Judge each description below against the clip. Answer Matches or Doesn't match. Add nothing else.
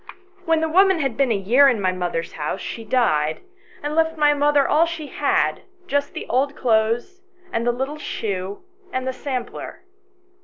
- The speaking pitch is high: Matches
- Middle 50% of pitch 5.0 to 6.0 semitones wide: Matches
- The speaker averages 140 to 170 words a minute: Doesn't match